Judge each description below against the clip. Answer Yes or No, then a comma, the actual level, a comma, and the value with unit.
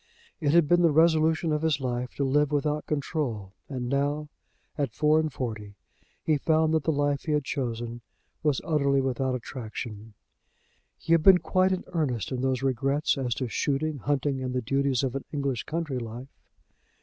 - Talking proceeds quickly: No, average, 180 wpm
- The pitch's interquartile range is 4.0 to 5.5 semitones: No, average, 3.4 semitones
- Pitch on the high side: No, medium, 140 Hz